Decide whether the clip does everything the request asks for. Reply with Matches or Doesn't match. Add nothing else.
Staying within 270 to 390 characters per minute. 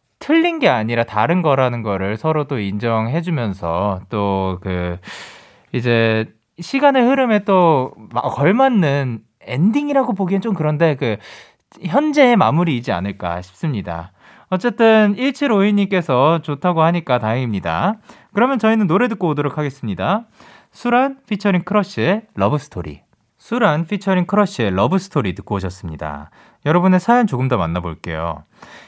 Matches